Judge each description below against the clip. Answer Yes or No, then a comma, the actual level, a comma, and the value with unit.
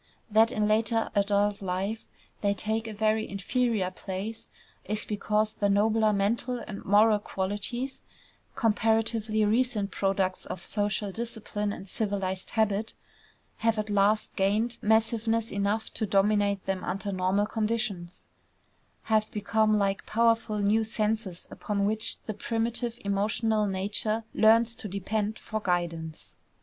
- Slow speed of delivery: Yes, slow, 130 wpm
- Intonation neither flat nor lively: No, narrow, 1.9 semitones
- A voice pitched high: Yes, high, 210 Hz